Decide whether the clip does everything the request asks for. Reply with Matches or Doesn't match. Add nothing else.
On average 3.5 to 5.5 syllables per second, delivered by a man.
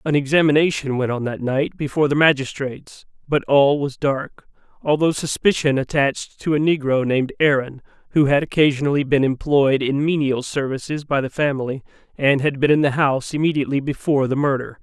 Doesn't match